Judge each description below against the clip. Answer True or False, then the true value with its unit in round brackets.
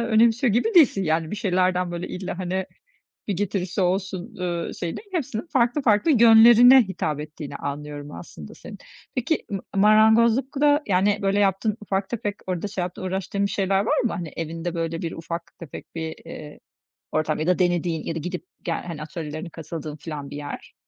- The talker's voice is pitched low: False (185 Hz)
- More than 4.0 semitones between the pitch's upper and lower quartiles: True (4.5 semitones)